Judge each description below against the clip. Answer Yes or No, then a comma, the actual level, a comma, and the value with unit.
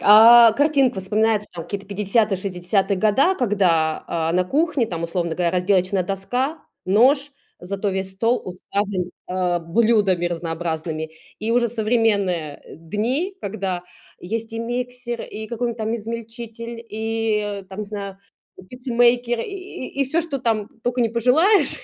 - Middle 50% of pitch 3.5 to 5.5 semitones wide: Yes, average, 4.2 semitones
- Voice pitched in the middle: No, high, 215 Hz